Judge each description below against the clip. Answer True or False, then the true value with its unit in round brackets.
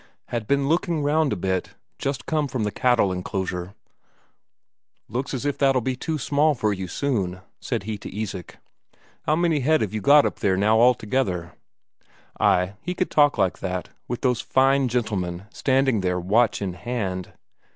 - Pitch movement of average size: False (6.6 semitones)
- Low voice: True (115 Hz)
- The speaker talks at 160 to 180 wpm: True (170 wpm)